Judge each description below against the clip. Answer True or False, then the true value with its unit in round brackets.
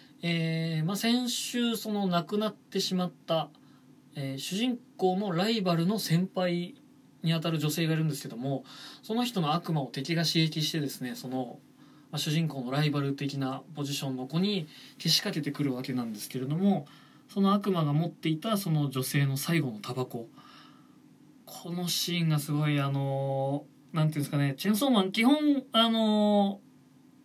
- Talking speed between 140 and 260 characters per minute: False (340 characters per minute)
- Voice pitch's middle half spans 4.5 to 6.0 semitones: True (5.6 semitones)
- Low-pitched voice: False (160 Hz)